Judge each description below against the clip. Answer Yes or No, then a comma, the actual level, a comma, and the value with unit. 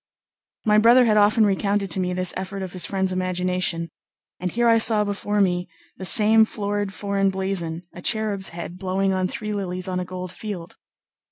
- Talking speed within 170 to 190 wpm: Yes, average, 185 wpm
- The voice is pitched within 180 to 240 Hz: Yes, high, 190 Hz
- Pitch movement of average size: No, narrow, 2.2 semitones